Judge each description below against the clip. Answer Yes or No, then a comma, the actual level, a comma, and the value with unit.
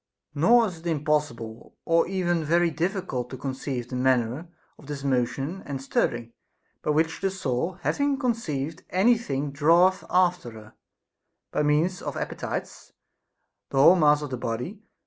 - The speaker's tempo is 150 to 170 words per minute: Yes, average, 155 wpm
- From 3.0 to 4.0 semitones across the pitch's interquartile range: No, average, 5.3 semitones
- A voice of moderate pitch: Yes, medium, 150 Hz